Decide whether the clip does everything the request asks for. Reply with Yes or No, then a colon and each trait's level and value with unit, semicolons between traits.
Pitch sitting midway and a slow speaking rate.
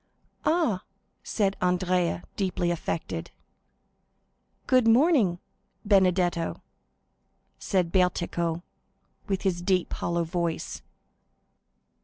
Yes: medium, 180 Hz; slow, 75 wpm